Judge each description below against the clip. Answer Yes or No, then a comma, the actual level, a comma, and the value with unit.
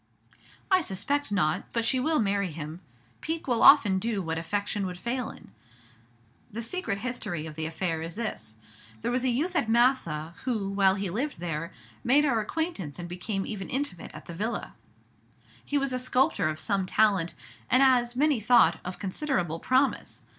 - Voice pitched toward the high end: Yes, high, 210 Hz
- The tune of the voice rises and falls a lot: Yes, wide, 6.4 semitones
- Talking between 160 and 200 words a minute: Yes, average, 175 wpm